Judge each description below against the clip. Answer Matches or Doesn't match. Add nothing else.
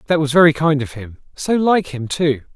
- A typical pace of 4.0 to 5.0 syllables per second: Doesn't match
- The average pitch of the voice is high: Doesn't match